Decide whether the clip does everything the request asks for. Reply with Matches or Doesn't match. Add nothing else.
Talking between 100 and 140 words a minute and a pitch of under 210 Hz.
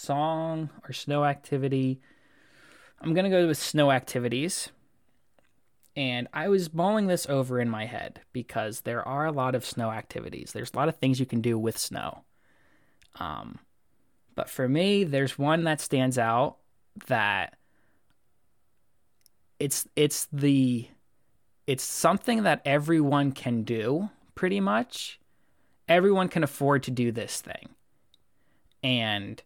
Matches